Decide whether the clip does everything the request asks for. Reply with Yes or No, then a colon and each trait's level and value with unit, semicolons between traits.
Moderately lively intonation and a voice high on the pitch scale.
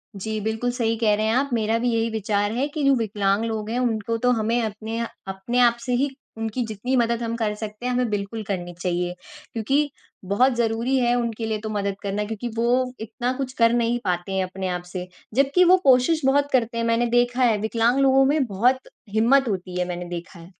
Yes: average, 3.0 semitones; high, 230 Hz